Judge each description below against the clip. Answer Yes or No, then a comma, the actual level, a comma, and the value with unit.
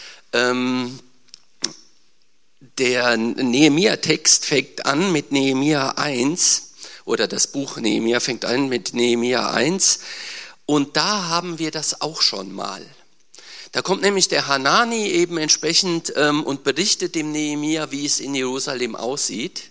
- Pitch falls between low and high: Yes, medium, 145 Hz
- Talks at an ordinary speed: No, slow, 120 wpm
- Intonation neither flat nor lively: Yes, average, 4.9 semitones